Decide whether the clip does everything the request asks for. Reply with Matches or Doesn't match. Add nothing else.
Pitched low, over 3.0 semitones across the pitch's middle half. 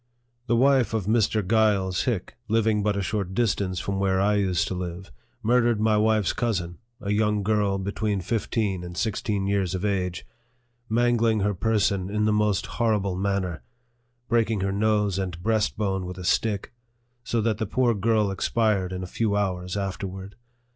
Doesn't match